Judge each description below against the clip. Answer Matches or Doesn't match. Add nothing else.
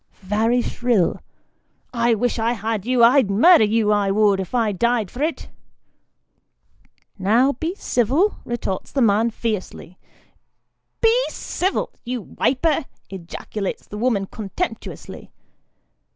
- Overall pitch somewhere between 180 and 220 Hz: Doesn't match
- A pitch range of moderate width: Matches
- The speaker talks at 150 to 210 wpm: Doesn't match